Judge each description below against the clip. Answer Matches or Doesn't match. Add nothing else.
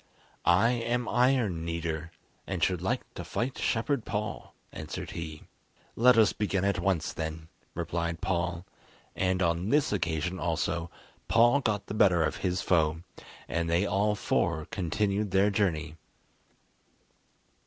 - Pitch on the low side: Matches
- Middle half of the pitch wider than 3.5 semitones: Matches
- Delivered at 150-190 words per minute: Doesn't match